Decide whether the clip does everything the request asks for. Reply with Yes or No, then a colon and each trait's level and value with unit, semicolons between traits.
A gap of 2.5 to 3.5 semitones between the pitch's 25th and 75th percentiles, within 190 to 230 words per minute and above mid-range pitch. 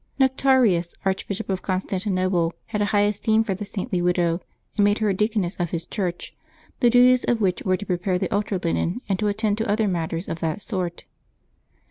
Yes: average, 3.2 semitones; average, 195 wpm; high, 195 Hz